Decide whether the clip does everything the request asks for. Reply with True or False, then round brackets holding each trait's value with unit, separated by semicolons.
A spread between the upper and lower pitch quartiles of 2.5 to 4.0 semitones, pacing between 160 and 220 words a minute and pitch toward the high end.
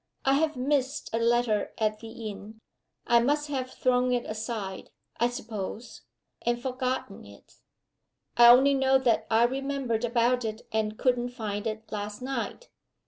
False (2.9 semitones; 150 wpm; 240 Hz)